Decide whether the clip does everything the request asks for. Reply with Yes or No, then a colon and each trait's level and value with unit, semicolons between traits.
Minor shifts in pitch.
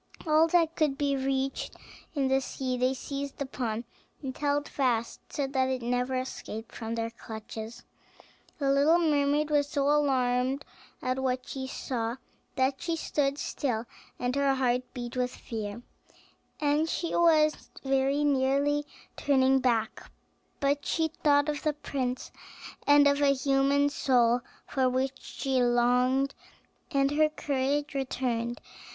Yes: narrow, 2.3 semitones